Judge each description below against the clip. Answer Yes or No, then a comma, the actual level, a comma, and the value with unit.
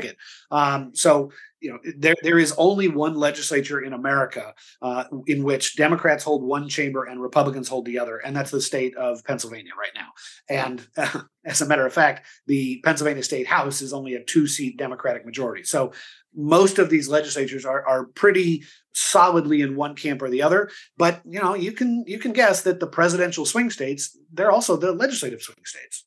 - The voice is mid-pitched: Yes, medium, 150 Hz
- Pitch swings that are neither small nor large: Yes, average, 4.0 semitones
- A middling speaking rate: Yes, average, 190 wpm